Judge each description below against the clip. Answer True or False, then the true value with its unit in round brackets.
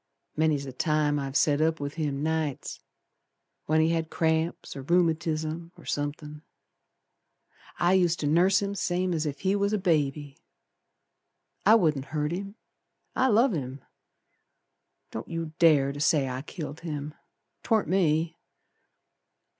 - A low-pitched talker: False (160 Hz)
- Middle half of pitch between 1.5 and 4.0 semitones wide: True (3.0 semitones)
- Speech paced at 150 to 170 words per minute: False (140 wpm)